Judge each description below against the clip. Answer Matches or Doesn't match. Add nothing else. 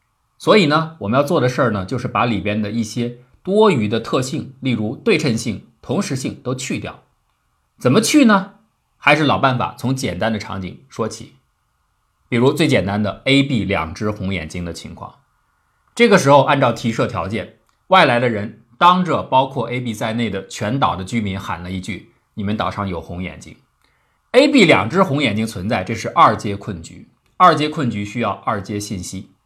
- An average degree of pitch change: Matches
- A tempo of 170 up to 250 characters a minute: Doesn't match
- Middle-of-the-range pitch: Doesn't match